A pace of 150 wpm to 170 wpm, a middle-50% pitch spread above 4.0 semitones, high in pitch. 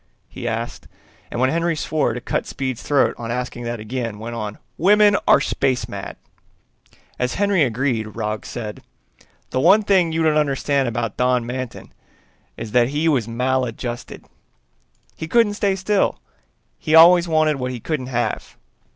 No: average, 160 wpm; average, 5.3 semitones; low, 130 Hz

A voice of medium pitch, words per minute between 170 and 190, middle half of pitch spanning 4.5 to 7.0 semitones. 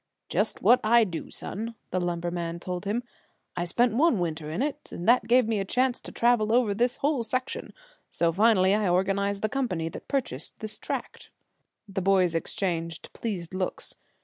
No: high, 200 Hz; average, 175 wpm; average, 5.2 semitones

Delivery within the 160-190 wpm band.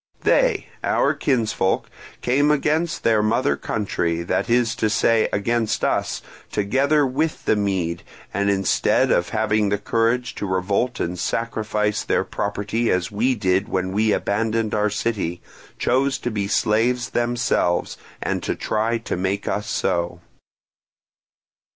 No: average, 140 wpm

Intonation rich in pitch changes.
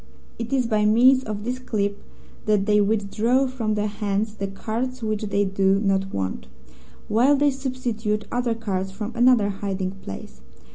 No: average, 3.3 semitones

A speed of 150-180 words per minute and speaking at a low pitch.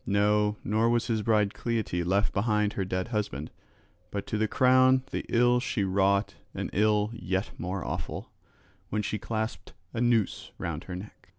Yes: average, 165 wpm; low, 105 Hz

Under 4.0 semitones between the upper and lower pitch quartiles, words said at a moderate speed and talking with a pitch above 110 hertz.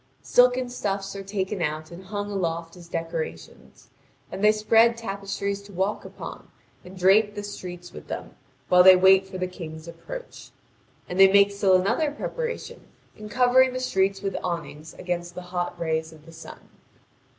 Yes: average, 3.1 semitones; average, 170 wpm; high, 190 Hz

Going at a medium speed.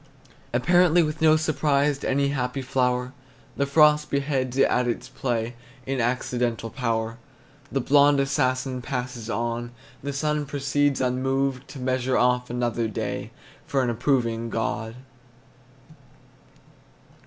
No: slow, 125 wpm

